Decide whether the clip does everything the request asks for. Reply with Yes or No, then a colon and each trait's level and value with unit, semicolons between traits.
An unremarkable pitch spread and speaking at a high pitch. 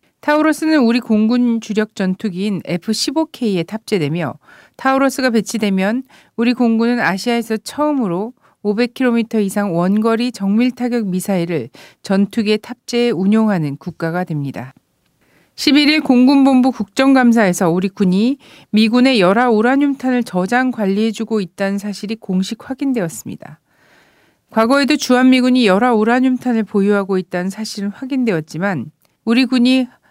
Yes: average, 4.3 semitones; high, 225 Hz